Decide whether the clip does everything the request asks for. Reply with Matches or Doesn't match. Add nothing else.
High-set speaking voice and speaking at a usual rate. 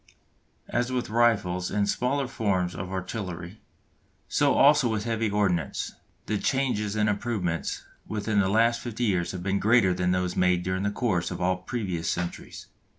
Doesn't match